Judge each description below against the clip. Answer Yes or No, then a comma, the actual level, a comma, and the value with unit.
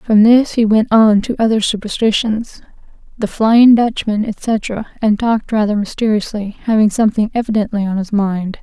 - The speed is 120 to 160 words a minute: Yes, average, 155 wpm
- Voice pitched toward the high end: Yes, high, 215 Hz